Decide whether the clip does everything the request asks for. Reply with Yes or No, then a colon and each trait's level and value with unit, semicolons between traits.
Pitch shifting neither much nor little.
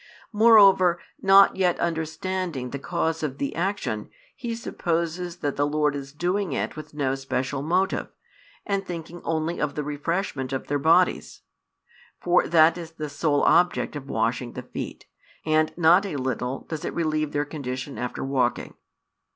Yes: average, 3.9 semitones